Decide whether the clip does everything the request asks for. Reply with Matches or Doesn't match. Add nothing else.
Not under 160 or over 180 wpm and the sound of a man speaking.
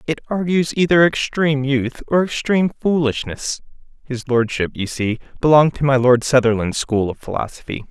Doesn't match